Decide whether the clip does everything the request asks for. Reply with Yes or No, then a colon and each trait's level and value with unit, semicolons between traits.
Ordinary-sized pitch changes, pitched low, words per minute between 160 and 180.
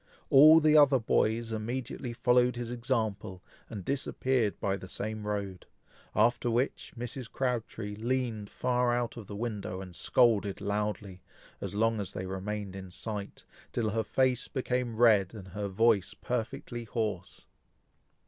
No: average, 3.2 semitones; low, 110 Hz; average, 145 wpm